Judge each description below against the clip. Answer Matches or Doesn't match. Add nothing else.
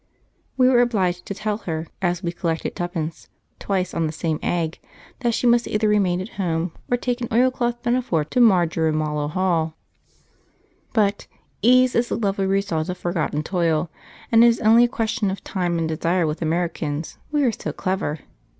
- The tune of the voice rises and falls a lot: Matches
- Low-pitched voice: Doesn't match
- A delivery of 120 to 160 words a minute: Doesn't match